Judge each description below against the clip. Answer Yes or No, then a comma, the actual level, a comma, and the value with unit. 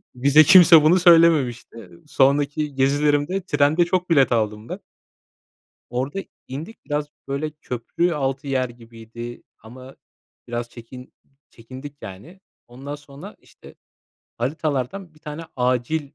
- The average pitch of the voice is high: No, medium, 140 Hz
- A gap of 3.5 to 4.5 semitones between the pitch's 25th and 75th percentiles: Yes, average, 3.9 semitones